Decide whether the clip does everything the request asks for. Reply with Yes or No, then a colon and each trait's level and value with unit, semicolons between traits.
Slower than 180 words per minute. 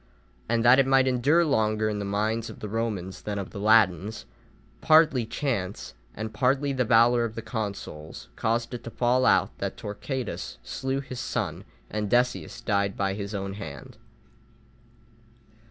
Yes: average, 160 wpm